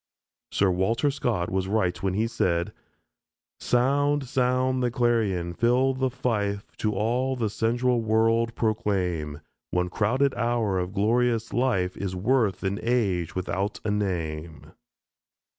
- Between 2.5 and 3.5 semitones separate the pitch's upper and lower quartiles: No, average, 4.6 semitones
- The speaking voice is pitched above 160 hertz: No, low, 110 Hz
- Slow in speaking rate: Yes, slow, 130 wpm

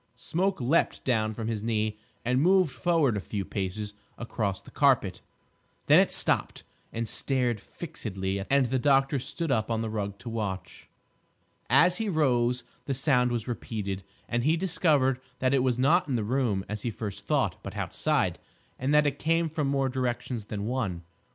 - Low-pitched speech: Yes, low, 125 Hz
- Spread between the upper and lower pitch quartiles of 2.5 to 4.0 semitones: No, average, 4.6 semitones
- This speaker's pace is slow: No, average, 175 wpm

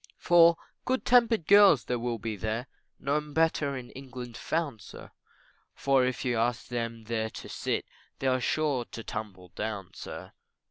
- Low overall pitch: Yes, low, 125 Hz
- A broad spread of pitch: No, average, 5.0 semitones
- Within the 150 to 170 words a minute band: Yes, average, 155 wpm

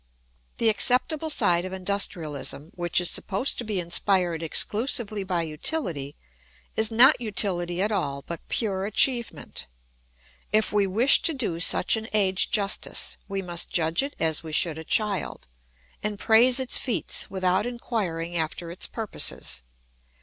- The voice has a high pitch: Yes, high, 195 Hz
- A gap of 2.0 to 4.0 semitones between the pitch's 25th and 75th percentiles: No, average, 4.5 semitones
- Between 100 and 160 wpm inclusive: Yes, average, 150 wpm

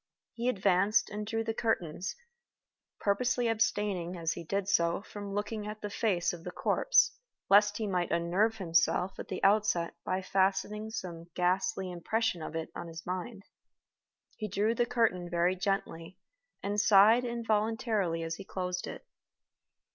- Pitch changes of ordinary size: Yes, average, 3.4 semitones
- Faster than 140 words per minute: Yes, average, 155 wpm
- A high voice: Yes, high, 195 Hz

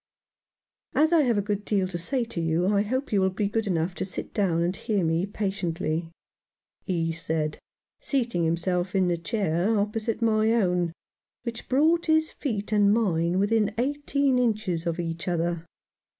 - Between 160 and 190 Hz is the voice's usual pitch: No, high, 200 Hz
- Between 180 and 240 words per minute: No, average, 170 wpm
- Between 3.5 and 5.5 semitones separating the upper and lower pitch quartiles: Yes, average, 4.7 semitones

